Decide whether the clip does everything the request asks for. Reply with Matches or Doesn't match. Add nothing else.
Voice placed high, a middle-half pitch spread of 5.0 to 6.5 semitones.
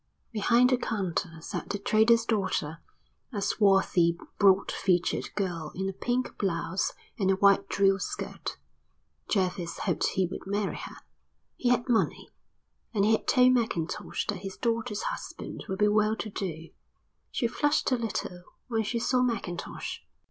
Doesn't match